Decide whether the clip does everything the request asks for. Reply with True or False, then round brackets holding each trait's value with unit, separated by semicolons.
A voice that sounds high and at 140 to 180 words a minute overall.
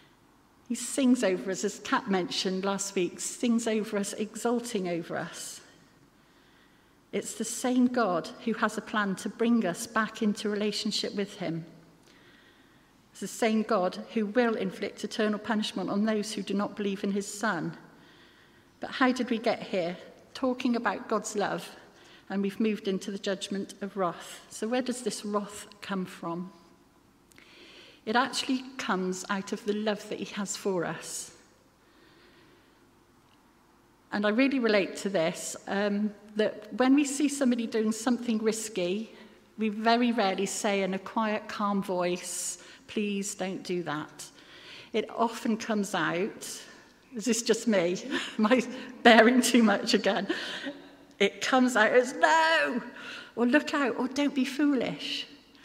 True (215 Hz; 150 wpm)